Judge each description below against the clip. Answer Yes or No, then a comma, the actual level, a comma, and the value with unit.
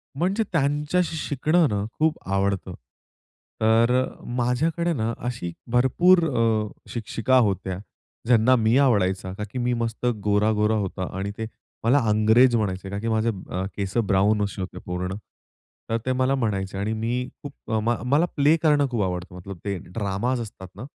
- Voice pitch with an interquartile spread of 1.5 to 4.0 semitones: No, average, 4.4 semitones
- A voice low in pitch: Yes, low, 115 Hz